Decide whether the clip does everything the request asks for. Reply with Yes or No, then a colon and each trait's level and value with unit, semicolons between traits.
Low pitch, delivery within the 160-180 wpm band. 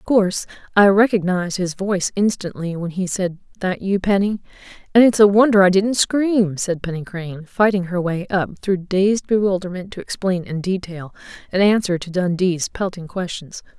No: high, 190 Hz; average, 175 wpm